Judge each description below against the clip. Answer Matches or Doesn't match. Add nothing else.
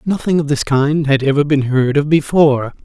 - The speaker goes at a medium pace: Doesn't match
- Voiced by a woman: Doesn't match